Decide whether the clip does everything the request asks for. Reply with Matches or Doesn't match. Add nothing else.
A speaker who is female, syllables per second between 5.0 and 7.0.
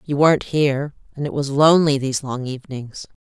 Matches